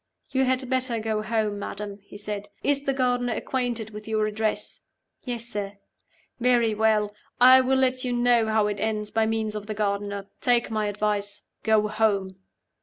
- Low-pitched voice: No, high, 220 Hz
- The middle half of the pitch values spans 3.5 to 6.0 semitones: No, average, 2.7 semitones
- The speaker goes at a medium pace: Yes, average, 175 wpm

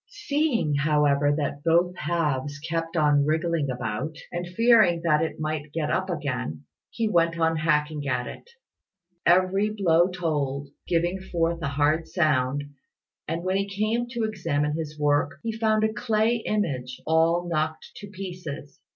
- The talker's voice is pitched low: No, medium, 165 Hz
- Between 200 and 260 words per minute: No, average, 150 wpm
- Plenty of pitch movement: No, average, 4.0 semitones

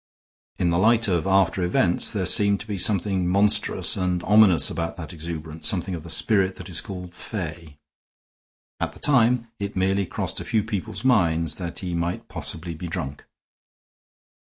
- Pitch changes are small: No, average, 3.2 semitones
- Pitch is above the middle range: No, very low, 95 Hz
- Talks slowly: No, average, 170 wpm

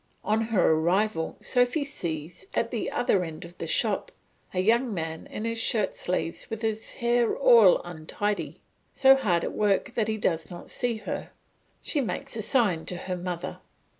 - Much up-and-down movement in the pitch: No, average, 4.9 semitones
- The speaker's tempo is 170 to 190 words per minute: Yes, average, 175 wpm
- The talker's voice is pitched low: No, high, 210 Hz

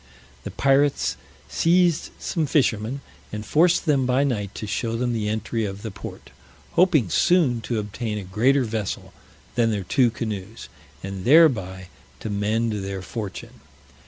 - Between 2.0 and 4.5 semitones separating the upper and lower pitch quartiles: No, average, 4.9 semitones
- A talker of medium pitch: No, low, 115 Hz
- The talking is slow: No, average, 150 wpm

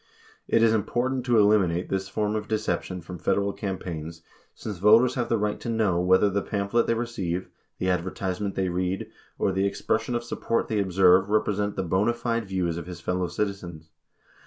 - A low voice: Yes, low, 100 Hz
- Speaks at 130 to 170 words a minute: No, average, 185 wpm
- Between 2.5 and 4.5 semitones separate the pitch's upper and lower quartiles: Yes, average, 3.2 semitones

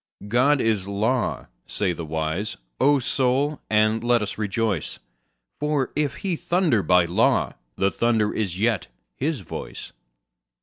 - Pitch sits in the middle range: No, low, 110 Hz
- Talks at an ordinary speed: No, slow, 130 wpm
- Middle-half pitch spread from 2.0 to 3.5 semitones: No, average, 5.3 semitones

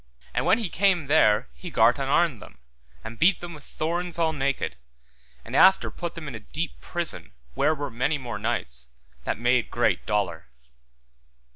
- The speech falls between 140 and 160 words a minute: No, average, 170 wpm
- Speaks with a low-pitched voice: No, medium, 145 Hz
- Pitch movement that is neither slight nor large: No, wide, 7.0 semitones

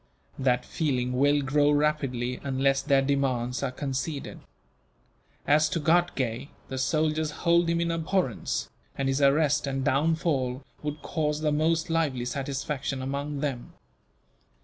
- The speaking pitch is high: No, medium, 140 Hz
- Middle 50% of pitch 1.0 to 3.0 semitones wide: Yes, narrow, 2.6 semitones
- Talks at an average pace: No, slow, 130 wpm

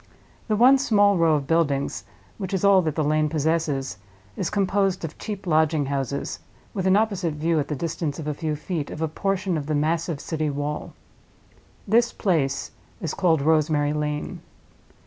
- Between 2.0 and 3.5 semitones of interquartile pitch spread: No, average, 4.1 semitones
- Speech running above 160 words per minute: Yes, average, 175 wpm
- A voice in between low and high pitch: Yes, medium, 160 Hz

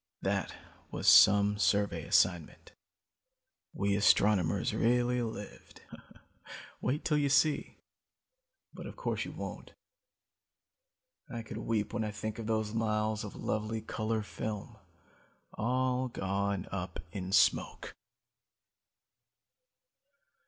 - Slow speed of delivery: Yes, slow, 105 wpm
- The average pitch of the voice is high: No, low, 110 Hz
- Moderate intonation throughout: No, narrow, 2.3 semitones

